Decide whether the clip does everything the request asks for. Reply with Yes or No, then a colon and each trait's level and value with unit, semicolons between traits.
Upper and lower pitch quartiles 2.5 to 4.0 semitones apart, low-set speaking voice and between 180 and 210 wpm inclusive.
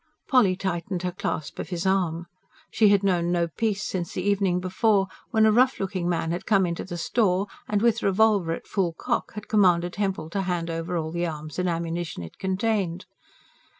No: average, 2.8 semitones; medium, 185 Hz; average, 195 wpm